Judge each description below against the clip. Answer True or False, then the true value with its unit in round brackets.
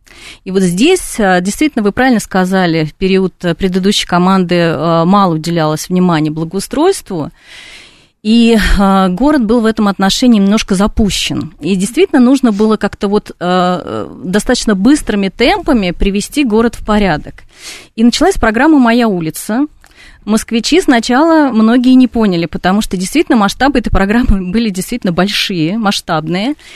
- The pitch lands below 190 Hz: False (210 Hz)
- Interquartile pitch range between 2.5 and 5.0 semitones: True (4.7 semitones)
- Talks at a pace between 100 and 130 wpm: True (125 wpm)